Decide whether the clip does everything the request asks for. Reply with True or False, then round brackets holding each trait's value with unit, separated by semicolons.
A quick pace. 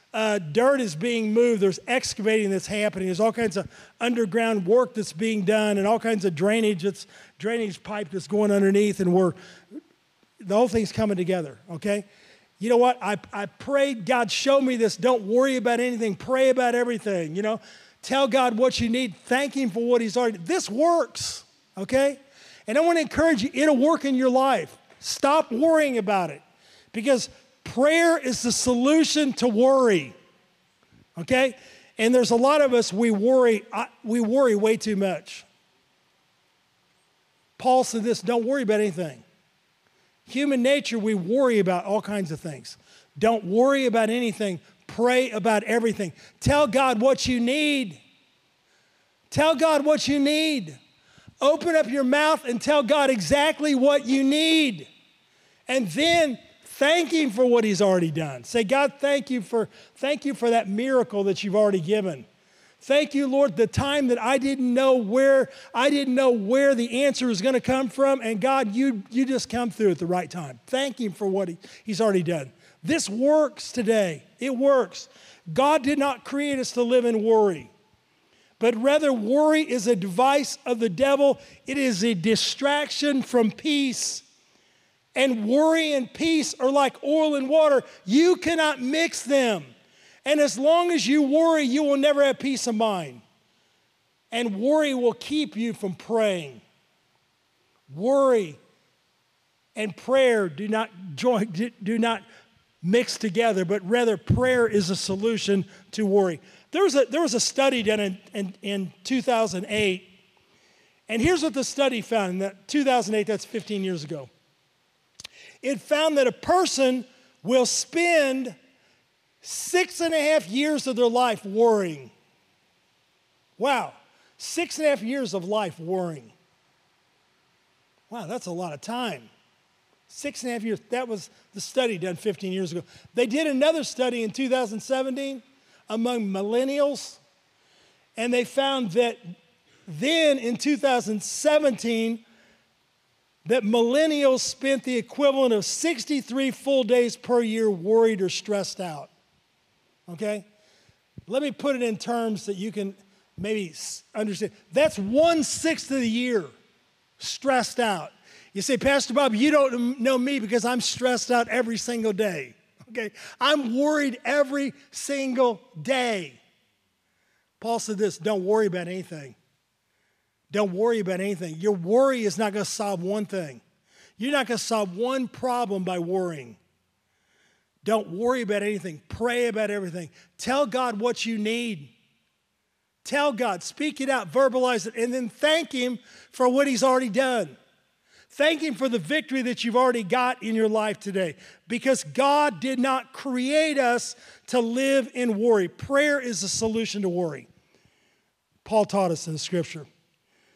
False (155 wpm)